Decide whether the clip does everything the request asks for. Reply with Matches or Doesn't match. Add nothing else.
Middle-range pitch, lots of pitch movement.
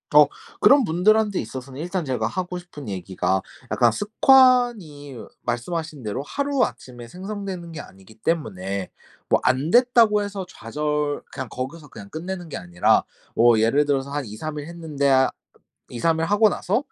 Matches